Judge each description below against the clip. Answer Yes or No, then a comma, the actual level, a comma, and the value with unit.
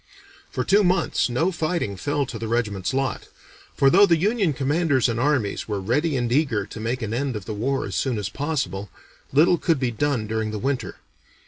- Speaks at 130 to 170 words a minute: No, fast, 205 wpm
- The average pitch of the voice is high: No, low, 130 Hz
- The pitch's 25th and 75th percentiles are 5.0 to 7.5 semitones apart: Yes, wide, 5.4 semitones